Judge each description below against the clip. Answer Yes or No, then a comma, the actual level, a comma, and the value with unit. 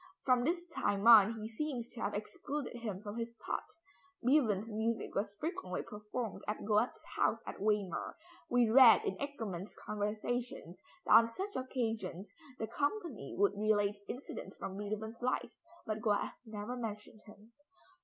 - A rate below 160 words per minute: Yes, average, 150 wpm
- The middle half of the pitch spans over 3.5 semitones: No, average, 3.0 semitones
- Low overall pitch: No, high, 220 Hz